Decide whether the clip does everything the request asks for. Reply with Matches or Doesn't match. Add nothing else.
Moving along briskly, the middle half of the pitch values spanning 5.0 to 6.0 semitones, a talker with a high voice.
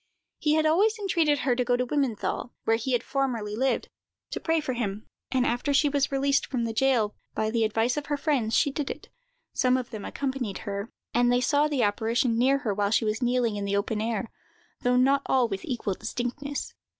Doesn't match